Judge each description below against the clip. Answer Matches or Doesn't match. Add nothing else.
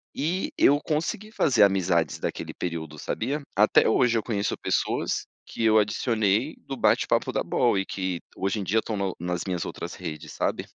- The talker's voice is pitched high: Doesn't match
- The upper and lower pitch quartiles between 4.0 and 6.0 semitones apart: Matches